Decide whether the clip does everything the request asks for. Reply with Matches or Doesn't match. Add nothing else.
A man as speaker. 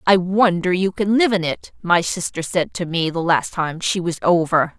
Doesn't match